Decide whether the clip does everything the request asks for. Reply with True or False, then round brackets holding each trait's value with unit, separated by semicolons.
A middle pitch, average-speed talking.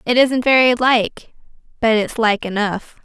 False (230 Hz; 160 wpm)